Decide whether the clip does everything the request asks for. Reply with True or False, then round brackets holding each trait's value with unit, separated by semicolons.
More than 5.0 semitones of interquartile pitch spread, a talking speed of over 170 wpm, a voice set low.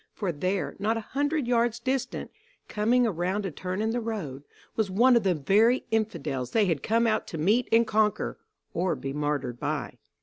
False (5.4 semitones; 190 wpm; 210 Hz)